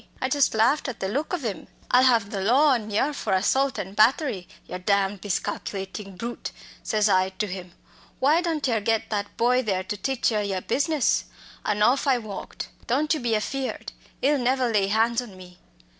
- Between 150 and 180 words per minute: No, average, 195 wpm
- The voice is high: Yes, high, 225 Hz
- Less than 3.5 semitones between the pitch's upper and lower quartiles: No, average, 4.7 semitones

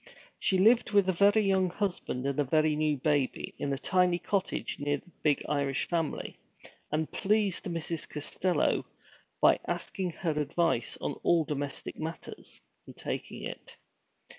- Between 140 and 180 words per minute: Yes, average, 150 wpm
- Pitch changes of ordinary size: Yes, average, 4.3 semitones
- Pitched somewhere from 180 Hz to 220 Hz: No, medium, 165 Hz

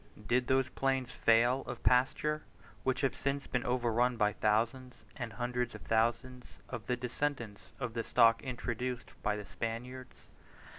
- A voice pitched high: No, low, 125 Hz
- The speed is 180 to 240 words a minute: No, average, 150 wpm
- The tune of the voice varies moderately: No, narrow, 1.9 semitones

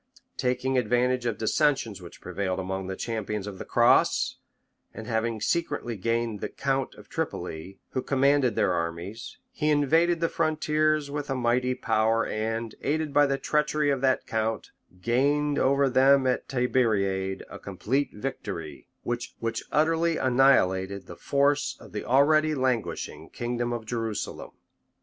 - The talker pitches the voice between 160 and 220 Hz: No, low, 125 Hz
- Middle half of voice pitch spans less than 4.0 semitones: No, average, 4.6 semitones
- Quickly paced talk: No, average, 145 wpm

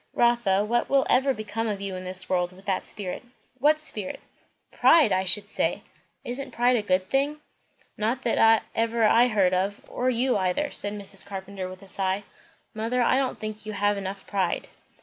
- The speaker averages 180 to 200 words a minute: Yes, average, 190 wpm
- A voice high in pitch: Yes, high, 210 Hz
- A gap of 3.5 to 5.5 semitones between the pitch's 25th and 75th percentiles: Yes, average, 4.0 semitones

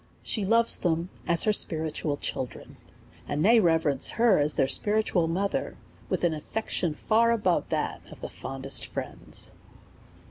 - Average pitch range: No, wide, 5.8 semitones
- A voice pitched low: No, medium, 175 Hz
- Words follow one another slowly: No, average, 150 wpm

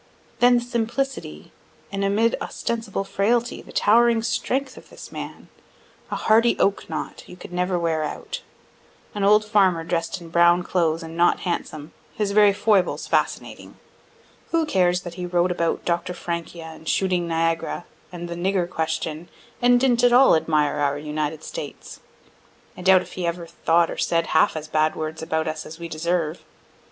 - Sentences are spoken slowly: No, average, 170 wpm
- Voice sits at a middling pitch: Yes, medium, 175 Hz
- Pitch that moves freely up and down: No, average, 4.2 semitones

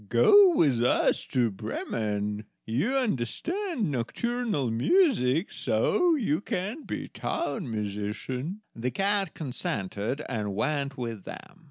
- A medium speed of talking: No, slow, 115 wpm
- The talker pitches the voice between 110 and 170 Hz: Yes, medium, 140 Hz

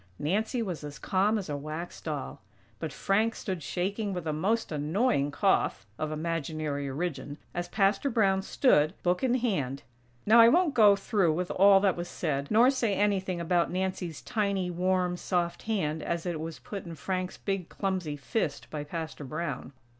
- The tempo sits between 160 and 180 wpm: Yes, average, 175 wpm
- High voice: No, medium, 180 Hz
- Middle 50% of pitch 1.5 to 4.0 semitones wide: No, average, 4.5 semitones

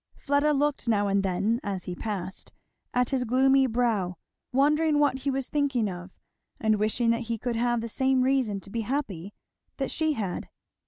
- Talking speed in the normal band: Yes, average, 180 wpm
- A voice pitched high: Yes, high, 240 Hz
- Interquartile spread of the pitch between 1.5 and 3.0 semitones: No, average, 4.7 semitones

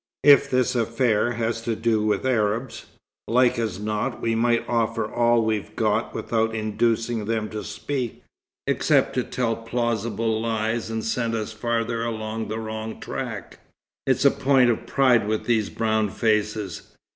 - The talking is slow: No, average, 155 wpm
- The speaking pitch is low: Yes, low, 115 Hz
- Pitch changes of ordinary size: No, narrow, 1.4 semitones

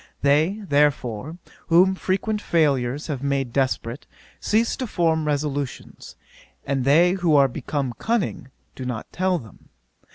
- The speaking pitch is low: No, medium, 145 Hz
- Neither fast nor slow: No, slow, 130 wpm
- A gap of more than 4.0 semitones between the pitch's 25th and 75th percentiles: Yes, average, 4.8 semitones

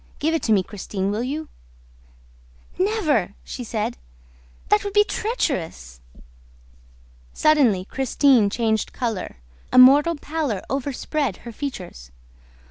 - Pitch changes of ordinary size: No, wide, 6.9 semitones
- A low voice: No, very high, 255 Hz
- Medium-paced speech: No, slow, 115 wpm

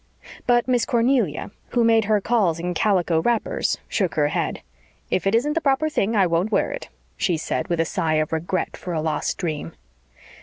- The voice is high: Yes, high, 195 Hz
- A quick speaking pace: No, average, 195 wpm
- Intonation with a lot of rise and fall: Yes, wide, 6.2 semitones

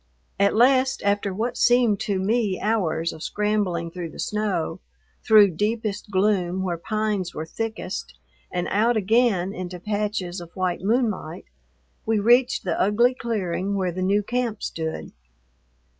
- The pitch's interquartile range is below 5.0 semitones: Yes, average, 3.3 semitones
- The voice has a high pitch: Yes, high, 205 Hz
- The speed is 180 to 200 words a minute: No, average, 145 wpm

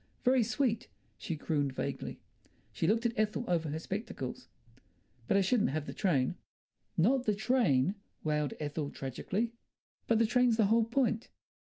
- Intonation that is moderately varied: No, wide, 7.3 semitones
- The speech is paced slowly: No, average, 155 wpm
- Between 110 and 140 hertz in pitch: No, high, 205 Hz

